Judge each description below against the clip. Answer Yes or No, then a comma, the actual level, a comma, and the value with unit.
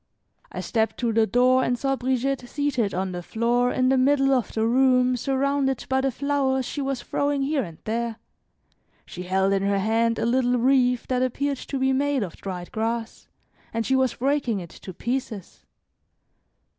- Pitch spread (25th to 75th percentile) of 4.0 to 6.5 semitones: No, average, 3.0 semitones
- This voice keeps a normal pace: Yes, average, 180 wpm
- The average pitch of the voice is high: Yes, very high, 250 Hz